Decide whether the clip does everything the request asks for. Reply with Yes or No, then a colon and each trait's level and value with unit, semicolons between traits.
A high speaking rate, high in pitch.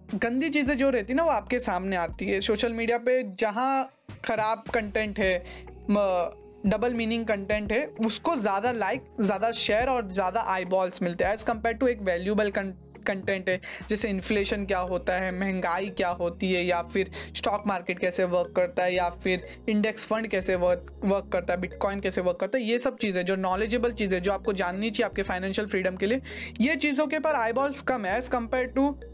Yes: fast, 200 wpm; high, 210 Hz